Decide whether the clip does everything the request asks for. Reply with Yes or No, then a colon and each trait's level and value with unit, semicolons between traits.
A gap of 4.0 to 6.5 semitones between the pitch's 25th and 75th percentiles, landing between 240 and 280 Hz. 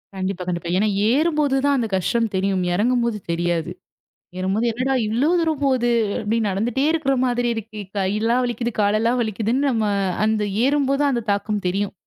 No: average, 4.3 semitones; high, 225 Hz